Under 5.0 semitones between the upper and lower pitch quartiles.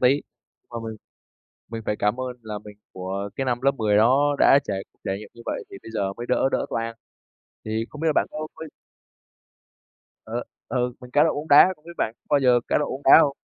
Yes: average, 4.6 semitones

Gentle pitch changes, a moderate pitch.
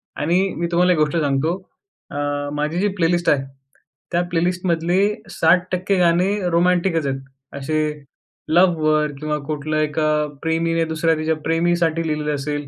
Yes: narrow, 2.2 semitones; medium, 165 Hz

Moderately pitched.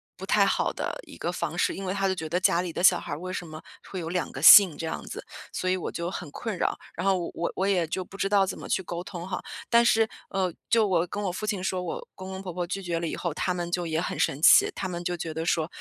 Yes: medium, 180 Hz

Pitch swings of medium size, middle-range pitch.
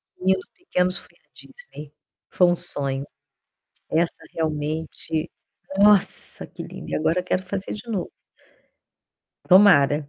Yes: average, 3.6 semitones; medium, 175 Hz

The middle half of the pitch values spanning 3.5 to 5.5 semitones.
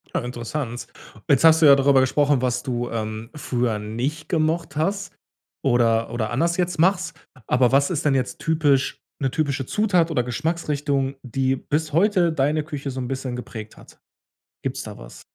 Yes: average, 4.4 semitones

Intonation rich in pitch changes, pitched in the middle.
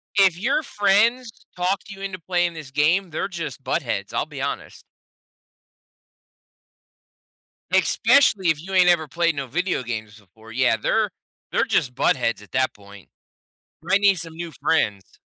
Yes: wide, 6.9 semitones; medium, 170 Hz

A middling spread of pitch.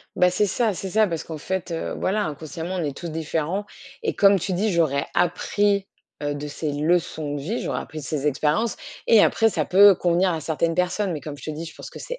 Yes: average, 4.1 semitones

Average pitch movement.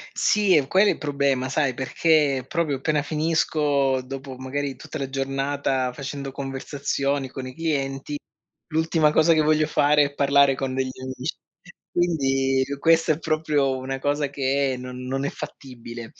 No: narrow, 2.3 semitones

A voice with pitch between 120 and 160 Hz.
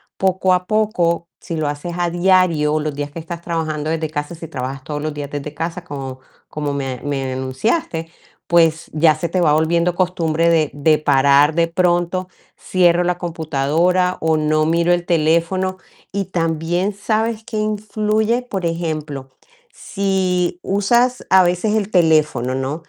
No: medium, 170 Hz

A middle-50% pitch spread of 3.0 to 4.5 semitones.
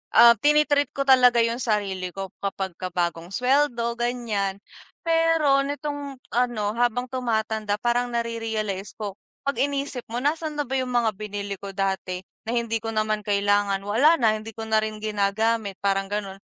Yes: average, 3.6 semitones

